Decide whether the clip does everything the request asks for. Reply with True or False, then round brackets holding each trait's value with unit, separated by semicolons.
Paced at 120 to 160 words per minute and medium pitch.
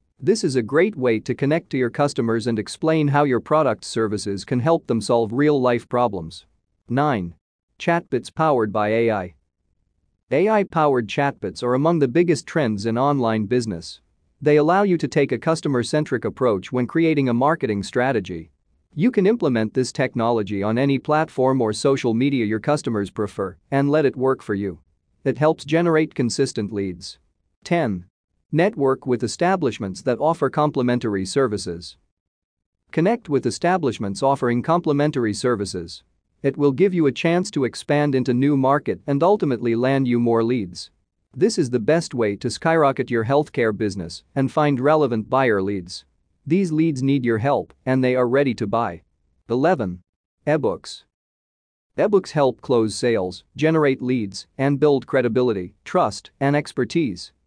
False (155 wpm; 125 Hz)